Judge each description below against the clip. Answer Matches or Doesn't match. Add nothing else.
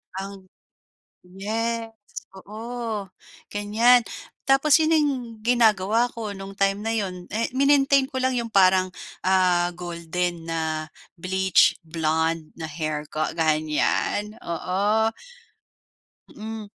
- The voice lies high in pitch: Matches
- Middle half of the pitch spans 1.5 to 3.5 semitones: Doesn't match